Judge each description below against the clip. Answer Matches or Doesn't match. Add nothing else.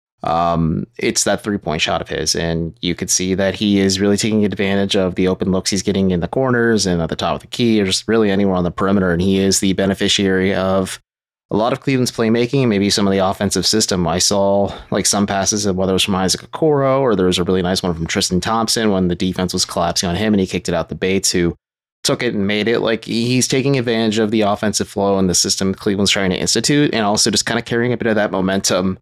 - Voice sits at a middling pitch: Doesn't match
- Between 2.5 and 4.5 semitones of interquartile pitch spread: Matches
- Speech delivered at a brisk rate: Matches